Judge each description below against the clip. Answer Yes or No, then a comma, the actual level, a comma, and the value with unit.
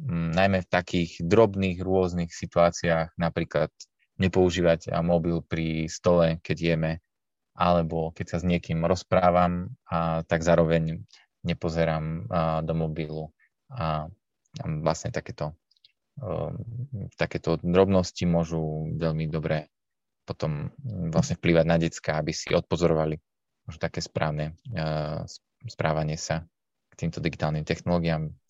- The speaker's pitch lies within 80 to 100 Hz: Yes, very low, 85 Hz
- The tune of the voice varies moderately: No, narrow, 1.9 semitones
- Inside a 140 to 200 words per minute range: No, average, 115 wpm